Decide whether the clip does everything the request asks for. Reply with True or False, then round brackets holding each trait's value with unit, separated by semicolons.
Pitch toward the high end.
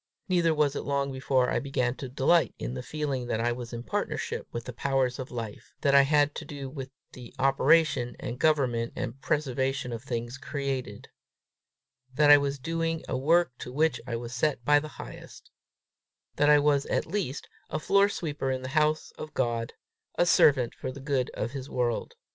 False (135 Hz)